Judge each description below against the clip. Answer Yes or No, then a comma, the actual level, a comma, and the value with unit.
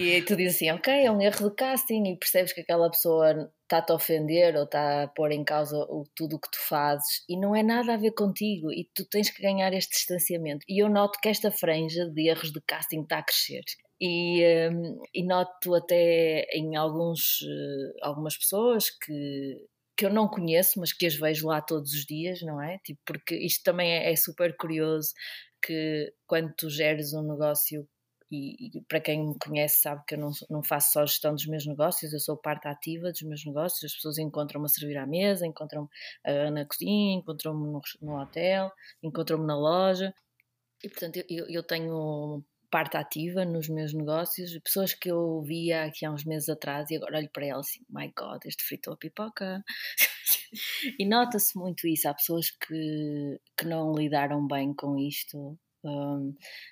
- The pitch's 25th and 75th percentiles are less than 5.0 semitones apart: Yes, average, 3.1 semitones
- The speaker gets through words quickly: Yes, fast, 195 wpm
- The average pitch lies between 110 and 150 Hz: No, medium, 160 Hz